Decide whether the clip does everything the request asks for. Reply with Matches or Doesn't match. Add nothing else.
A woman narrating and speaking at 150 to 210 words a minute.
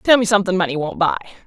Doesn't match